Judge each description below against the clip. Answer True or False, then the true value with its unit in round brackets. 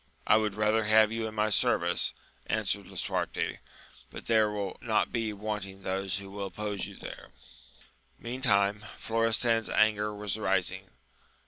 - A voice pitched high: False (105 Hz)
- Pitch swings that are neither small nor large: False (1.6 semitones)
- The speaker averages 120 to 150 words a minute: True (140 wpm)